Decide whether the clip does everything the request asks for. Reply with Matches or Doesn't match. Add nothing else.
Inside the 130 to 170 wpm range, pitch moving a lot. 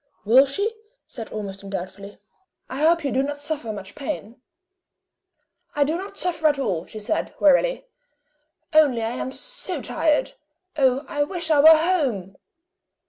Matches